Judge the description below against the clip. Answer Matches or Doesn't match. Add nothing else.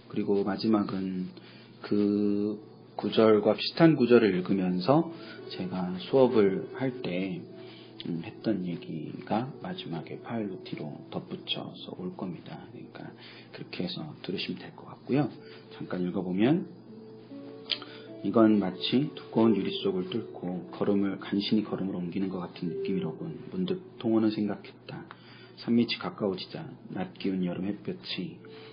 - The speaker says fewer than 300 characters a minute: Matches